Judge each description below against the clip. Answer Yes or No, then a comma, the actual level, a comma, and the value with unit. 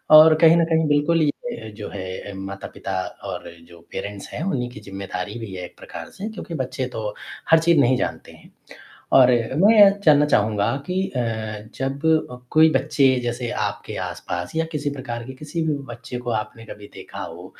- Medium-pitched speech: No, low, 130 Hz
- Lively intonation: Yes, wide, 6.9 semitones